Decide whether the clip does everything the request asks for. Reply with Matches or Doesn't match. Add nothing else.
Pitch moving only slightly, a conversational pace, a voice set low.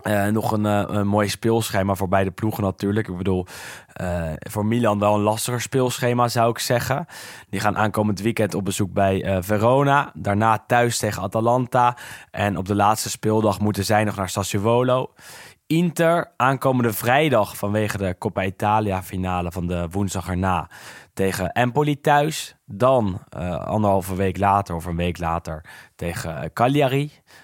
Doesn't match